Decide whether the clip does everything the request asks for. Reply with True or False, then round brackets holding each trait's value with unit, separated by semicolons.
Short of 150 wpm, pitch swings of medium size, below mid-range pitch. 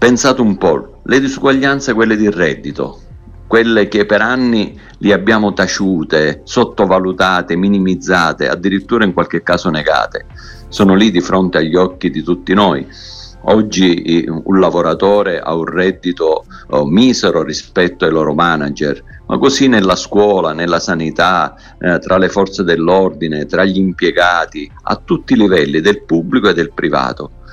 True (140 wpm; 3.5 semitones; 95 Hz)